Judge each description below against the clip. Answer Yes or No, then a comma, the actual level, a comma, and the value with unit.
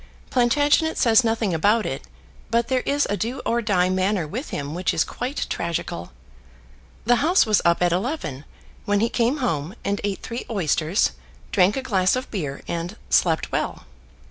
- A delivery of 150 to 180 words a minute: Yes, average, 170 wpm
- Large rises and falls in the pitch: Yes, wide, 5.7 semitones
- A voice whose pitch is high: Yes, high, 205 Hz